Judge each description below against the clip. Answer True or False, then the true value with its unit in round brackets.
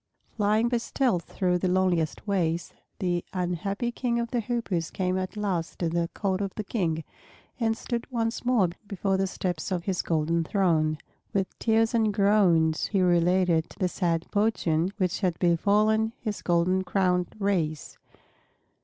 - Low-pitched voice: False (185 Hz)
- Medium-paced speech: True (155 wpm)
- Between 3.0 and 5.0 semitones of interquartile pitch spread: True (3.7 semitones)